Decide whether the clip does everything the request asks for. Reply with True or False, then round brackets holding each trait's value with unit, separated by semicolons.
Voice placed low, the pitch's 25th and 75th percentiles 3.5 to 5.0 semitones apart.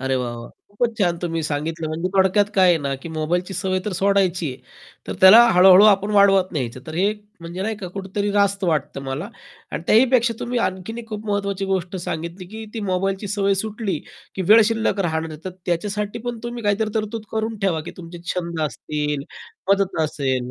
False (190 Hz; 3.9 semitones)